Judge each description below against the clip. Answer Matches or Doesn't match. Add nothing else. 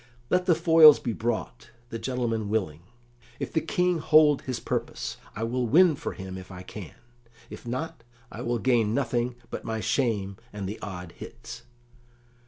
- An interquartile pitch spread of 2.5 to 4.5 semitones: Doesn't match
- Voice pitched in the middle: Doesn't match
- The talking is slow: Doesn't match